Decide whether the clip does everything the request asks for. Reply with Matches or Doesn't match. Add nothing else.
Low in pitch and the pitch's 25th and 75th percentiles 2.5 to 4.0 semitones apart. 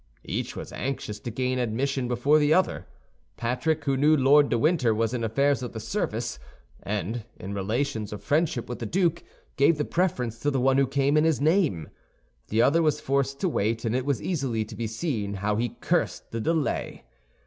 Doesn't match